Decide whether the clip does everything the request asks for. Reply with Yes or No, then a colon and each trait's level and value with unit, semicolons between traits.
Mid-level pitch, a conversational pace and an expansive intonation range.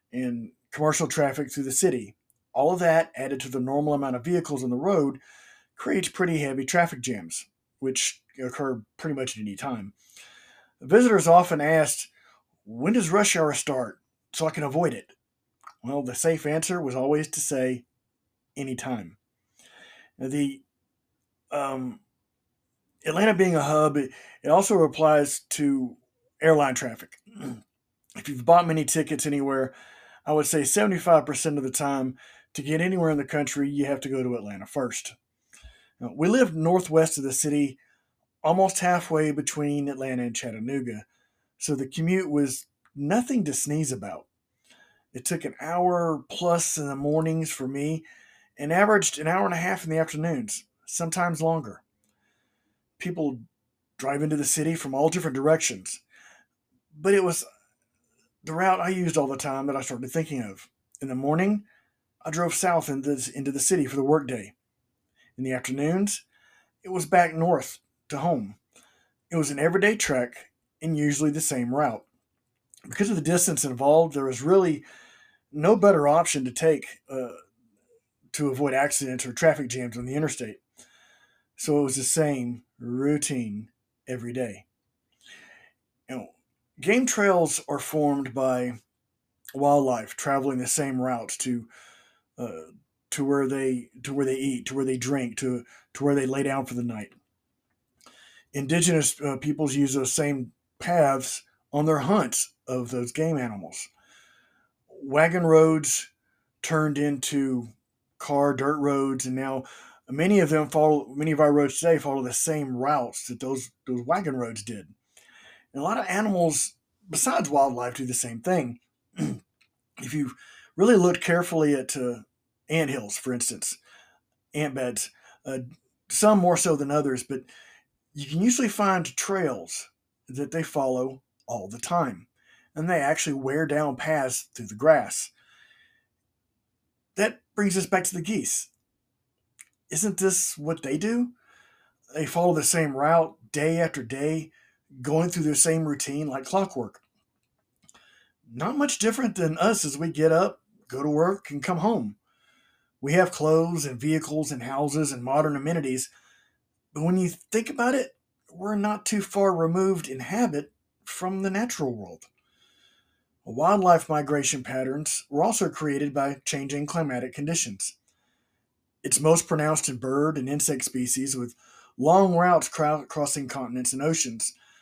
No: medium, 145 Hz; average, 150 wpm; average, 4.1 semitones